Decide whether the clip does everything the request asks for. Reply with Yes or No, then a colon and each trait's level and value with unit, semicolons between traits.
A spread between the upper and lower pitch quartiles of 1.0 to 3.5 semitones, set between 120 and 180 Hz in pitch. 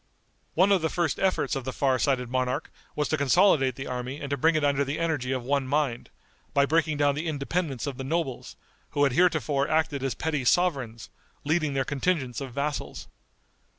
Yes: average, 3.2 semitones; medium, 140 Hz